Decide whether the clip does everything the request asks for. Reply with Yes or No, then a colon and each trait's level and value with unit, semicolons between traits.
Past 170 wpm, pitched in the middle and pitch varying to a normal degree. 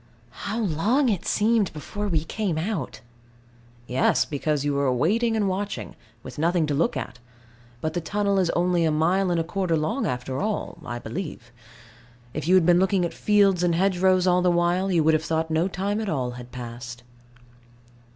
Yes: average, 190 wpm; medium, 175 Hz; average, 4.4 semitones